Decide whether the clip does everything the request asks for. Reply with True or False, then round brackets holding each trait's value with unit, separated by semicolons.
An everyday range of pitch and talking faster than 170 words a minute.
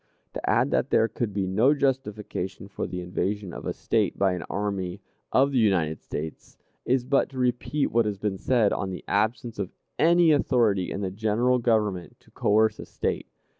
True (4.5 semitones; 190 wpm)